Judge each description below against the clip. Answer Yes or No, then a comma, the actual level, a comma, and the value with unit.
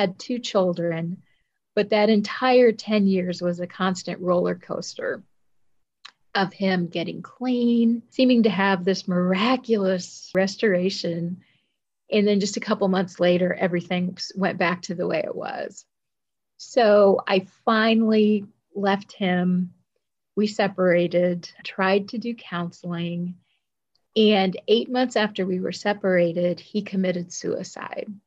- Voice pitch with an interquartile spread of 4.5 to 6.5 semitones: No, average, 3.1 semitones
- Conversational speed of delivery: No, slow, 125 wpm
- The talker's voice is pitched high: Yes, high, 195 Hz